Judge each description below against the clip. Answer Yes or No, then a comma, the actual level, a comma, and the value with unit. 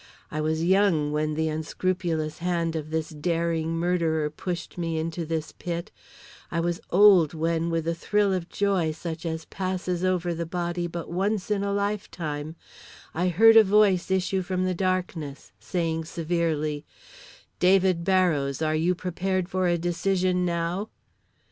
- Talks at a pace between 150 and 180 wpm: Yes, average, 155 wpm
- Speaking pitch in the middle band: Yes, medium, 170 Hz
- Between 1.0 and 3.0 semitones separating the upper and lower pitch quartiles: Yes, narrow, 2.4 semitones